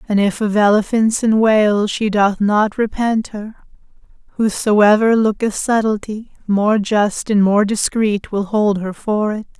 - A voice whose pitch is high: Yes, high, 210 Hz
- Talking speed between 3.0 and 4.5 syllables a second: Yes, 4.0 syllables/s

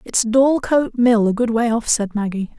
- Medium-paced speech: No, fast, 210 wpm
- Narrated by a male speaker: No, female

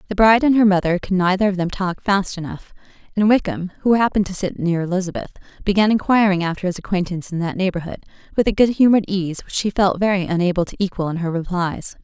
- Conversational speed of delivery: No, fast, 215 wpm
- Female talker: Yes, female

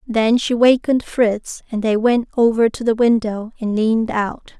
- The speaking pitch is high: Yes, high, 225 Hz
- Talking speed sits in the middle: Yes, average, 185 wpm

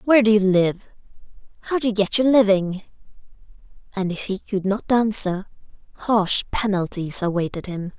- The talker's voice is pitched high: Yes, high, 200 Hz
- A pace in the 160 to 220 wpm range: No, average, 150 wpm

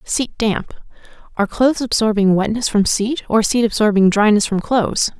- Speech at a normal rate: Yes, average, 160 wpm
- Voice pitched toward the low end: No, high, 220 Hz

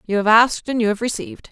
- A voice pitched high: Yes, high, 225 Hz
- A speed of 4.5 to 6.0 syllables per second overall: No, 7.1 syllables/s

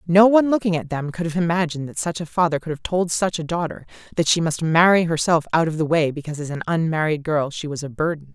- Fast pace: Yes, fast, 260 wpm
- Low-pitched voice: No, medium, 165 Hz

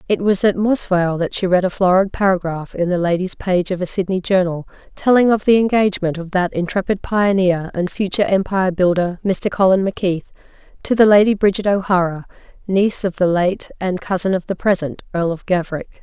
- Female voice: Yes, female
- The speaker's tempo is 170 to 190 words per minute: Yes, average, 185 wpm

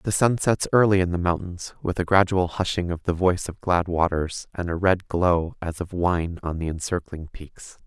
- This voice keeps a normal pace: No, fast, 215 wpm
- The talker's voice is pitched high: No, very low, 90 Hz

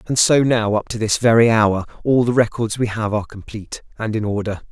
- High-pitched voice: No, low, 110 Hz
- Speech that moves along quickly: Yes, fast, 230 wpm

